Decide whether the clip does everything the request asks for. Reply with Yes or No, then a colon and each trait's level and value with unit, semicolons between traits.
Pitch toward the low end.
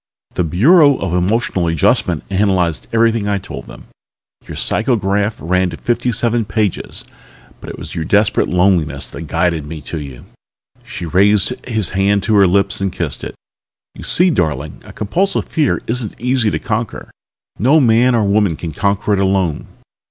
Yes: low, 100 Hz